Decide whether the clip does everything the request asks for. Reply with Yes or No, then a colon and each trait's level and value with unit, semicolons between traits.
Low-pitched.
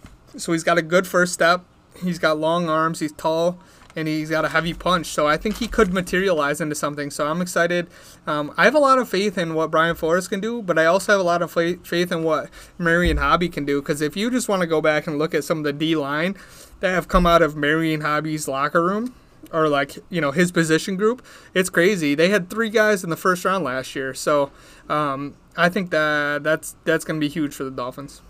No: medium, 165 Hz